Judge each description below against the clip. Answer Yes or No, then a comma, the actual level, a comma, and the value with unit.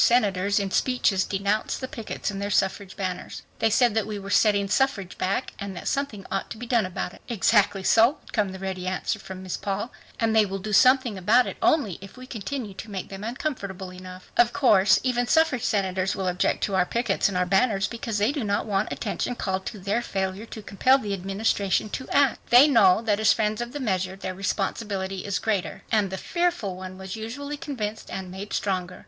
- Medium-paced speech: No, fast, 215 wpm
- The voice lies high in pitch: Yes, high, 205 Hz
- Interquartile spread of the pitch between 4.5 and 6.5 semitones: No, average, 3.6 semitones